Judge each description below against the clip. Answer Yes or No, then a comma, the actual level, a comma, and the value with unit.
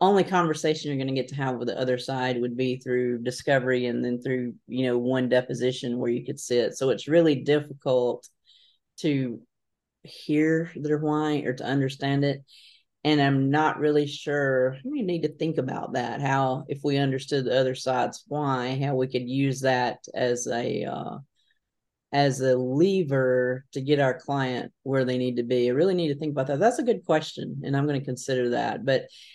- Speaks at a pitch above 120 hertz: Yes, low, 135 Hz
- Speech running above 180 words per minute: Yes, average, 195 wpm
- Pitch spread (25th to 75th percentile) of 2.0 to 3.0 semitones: Yes, average, 2.7 semitones